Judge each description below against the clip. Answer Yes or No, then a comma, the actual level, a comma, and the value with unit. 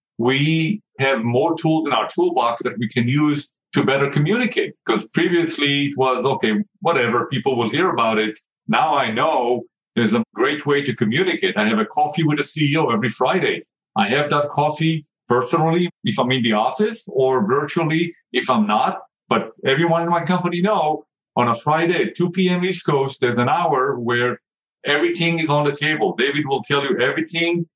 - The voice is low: No, medium, 150 Hz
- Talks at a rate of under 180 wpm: No, average, 185 wpm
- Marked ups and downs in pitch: No, average, 4.3 semitones